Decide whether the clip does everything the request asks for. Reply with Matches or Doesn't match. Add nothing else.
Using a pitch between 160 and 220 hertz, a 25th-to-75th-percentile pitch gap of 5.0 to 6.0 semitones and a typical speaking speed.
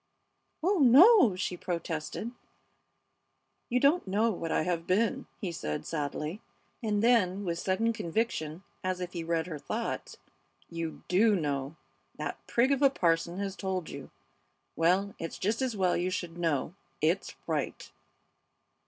Matches